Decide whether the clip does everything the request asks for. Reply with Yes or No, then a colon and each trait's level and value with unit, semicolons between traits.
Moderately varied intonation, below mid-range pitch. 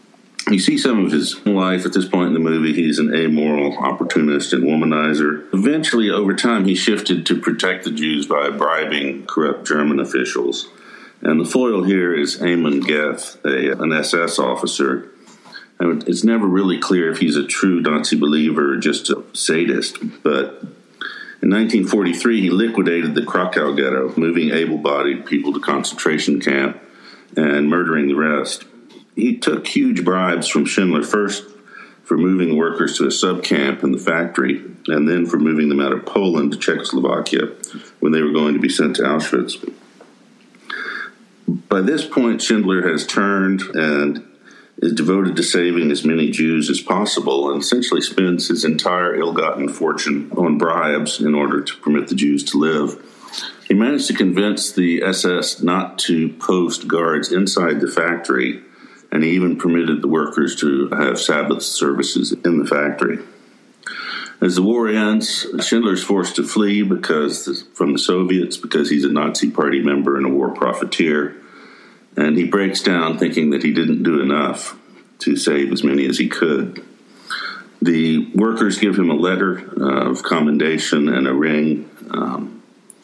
Yes: average, 4.2 semitones; very low, 80 Hz